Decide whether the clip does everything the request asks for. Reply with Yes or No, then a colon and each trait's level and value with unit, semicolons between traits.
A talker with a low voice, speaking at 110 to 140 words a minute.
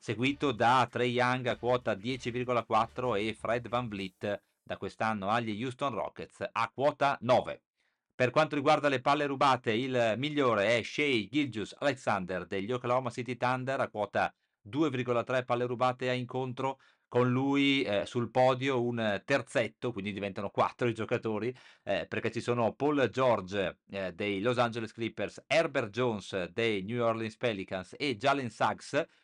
No: low, 120 Hz; average, 150 wpm